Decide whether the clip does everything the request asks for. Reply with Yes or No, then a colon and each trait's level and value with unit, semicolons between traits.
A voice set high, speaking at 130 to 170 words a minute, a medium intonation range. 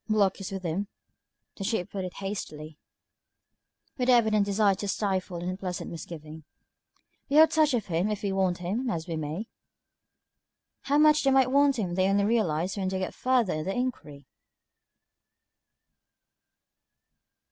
Yes: high, 195 Hz; average, 160 wpm; average, 4.6 semitones